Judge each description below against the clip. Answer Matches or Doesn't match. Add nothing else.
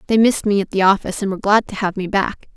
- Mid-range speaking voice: Doesn't match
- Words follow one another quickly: Matches